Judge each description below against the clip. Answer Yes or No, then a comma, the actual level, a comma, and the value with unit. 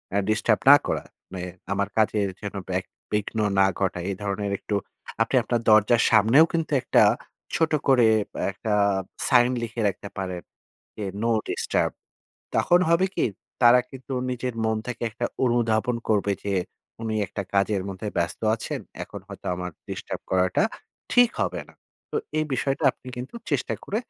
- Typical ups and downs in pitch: Yes, average, 3.9 semitones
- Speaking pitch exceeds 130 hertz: No, low, 110 Hz